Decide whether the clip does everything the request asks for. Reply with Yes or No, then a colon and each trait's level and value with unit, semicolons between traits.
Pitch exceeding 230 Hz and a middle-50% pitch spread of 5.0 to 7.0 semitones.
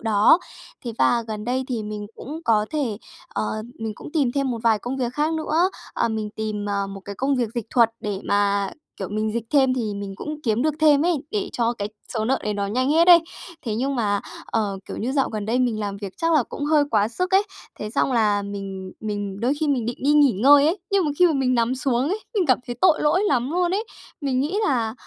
Yes: high, 240 Hz; wide, 5.6 semitones